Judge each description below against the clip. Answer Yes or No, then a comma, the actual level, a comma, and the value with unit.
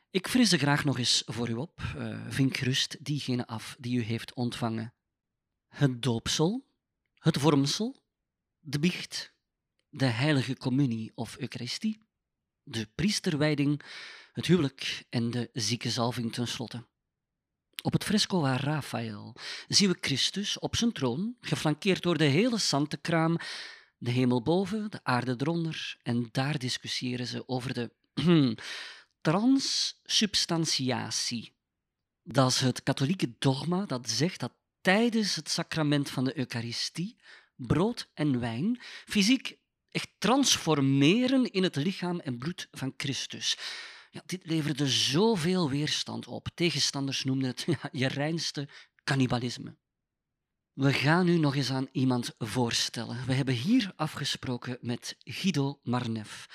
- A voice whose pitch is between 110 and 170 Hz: Yes, medium, 140 Hz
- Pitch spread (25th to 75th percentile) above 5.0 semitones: Yes, wide, 5.4 semitones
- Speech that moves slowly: Yes, slow, 125 wpm